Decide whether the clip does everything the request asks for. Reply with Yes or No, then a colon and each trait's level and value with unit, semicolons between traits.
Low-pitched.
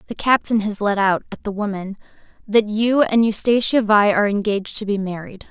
No: high, 210 Hz